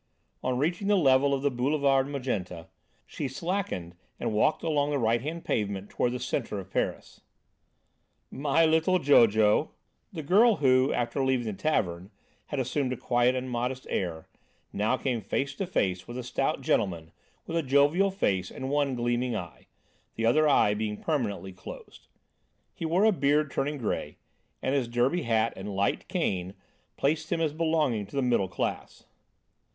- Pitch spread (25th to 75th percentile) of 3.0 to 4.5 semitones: No, wide, 5.4 semitones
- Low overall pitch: Yes, low, 130 Hz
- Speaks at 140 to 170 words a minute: Yes, average, 165 wpm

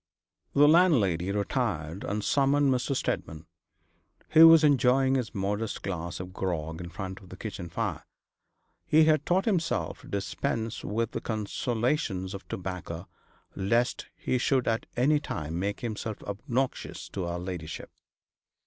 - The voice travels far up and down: Yes, wide, 6.3 semitones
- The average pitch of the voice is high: No, low, 105 Hz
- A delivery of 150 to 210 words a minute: No, average, 140 wpm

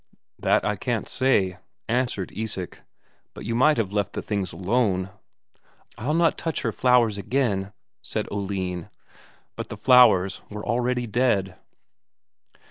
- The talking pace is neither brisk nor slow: No, slow, 130 wpm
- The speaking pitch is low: Yes, low, 105 Hz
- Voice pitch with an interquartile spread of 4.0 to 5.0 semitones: Yes, average, 4.5 semitones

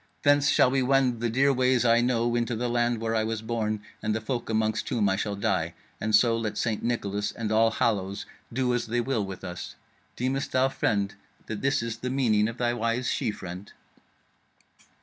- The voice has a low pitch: Yes, low, 115 Hz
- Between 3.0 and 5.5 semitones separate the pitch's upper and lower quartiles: No, narrow, 2.5 semitones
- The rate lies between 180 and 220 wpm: Yes, fast, 205 wpm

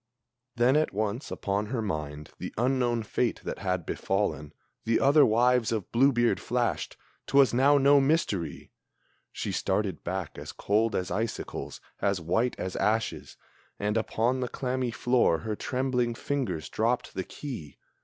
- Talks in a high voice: No, low, 115 Hz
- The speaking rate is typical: Yes, average, 150 wpm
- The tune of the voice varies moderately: Yes, average, 4.3 semitones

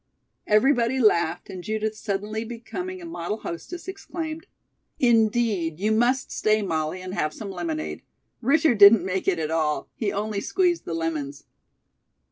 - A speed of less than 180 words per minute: Yes, average, 150 wpm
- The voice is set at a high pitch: Yes, high, 215 Hz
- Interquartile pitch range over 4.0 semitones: Yes, wide, 5.6 semitones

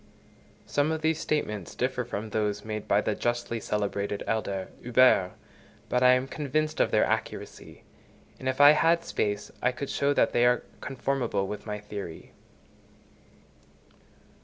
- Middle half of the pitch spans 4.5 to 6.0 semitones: Yes, average, 4.9 semitones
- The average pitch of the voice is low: Yes, low, 120 Hz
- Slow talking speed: No, average, 150 wpm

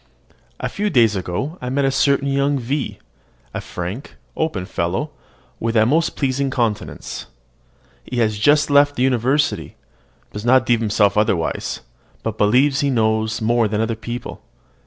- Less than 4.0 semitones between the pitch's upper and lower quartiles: No, average, 4.3 semitones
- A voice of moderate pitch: No, low, 120 Hz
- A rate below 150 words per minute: No, average, 155 wpm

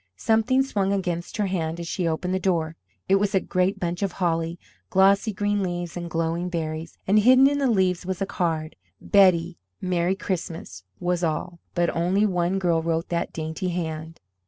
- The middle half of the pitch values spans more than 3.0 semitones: No, narrow, 2.6 semitones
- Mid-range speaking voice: Yes, medium, 180 Hz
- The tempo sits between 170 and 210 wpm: Yes, average, 180 wpm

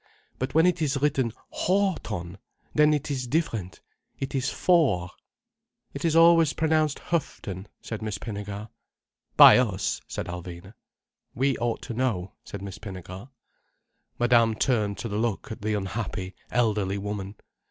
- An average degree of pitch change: No, wide, 5.9 semitones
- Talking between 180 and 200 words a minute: No, average, 145 wpm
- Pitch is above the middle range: No, low, 115 Hz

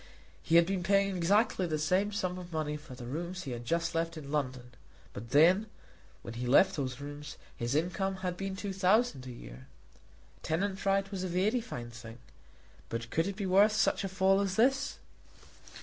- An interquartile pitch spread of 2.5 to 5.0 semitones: No, wide, 5.5 semitones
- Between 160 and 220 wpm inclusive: Yes, average, 195 wpm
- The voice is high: No, medium, 175 Hz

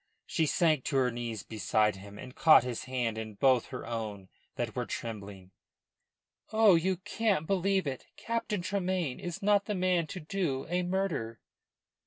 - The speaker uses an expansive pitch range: Yes, wide, 8.7 semitones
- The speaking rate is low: No, average, 165 wpm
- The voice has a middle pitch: Yes, medium, 155 Hz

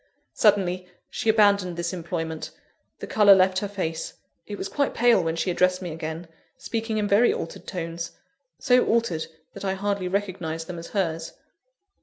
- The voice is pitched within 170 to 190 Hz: Yes, medium, 185 Hz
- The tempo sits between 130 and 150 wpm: No, average, 165 wpm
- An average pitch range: Yes, average, 3.5 semitones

